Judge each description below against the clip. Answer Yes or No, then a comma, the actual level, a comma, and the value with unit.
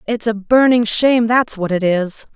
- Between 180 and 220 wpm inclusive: Yes, fast, 205 wpm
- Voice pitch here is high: Yes, high, 220 Hz